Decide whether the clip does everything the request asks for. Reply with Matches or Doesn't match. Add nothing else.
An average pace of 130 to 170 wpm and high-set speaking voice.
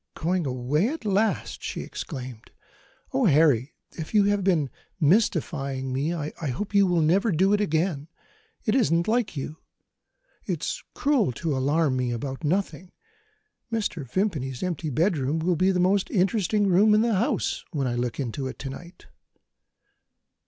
Doesn't match